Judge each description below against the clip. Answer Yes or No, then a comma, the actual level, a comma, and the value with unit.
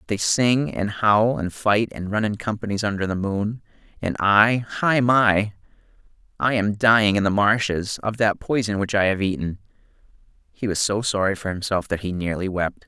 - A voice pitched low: Yes, low, 105 Hz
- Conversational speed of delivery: Yes, average, 175 wpm